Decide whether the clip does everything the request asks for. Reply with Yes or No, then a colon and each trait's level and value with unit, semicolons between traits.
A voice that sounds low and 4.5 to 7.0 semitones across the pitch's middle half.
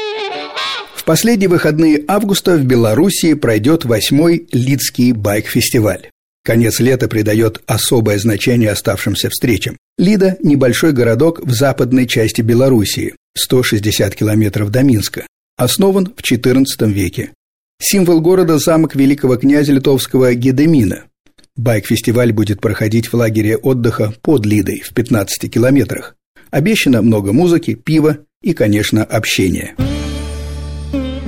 Yes: low, 125 Hz; average, 5.3 semitones